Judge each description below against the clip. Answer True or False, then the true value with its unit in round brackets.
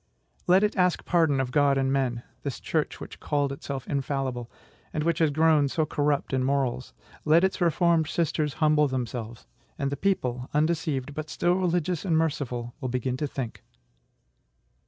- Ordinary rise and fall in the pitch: True (3.5 semitones)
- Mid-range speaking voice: True (145 Hz)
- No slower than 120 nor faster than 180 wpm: True (165 wpm)